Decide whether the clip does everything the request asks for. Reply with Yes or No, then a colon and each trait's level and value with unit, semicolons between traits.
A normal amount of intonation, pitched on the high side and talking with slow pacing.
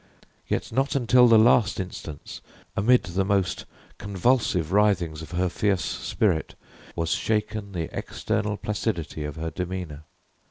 No: average, 4.2 semitones; very low, 95 Hz; slow, 130 wpm